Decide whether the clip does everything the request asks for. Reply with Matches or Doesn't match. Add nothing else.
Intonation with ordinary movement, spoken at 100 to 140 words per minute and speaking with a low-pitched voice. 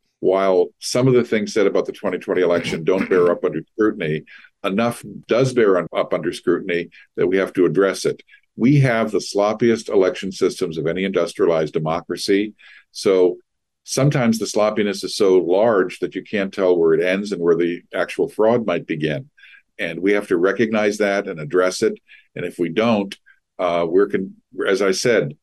Doesn't match